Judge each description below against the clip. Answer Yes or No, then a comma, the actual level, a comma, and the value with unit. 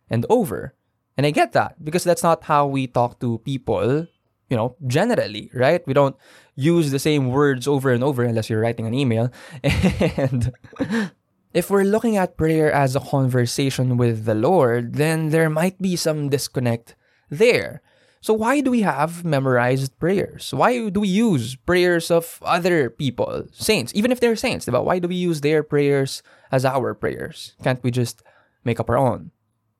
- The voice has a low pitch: No, medium, 145 Hz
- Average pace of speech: Yes, average, 175 wpm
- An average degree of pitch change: No, wide, 5.9 semitones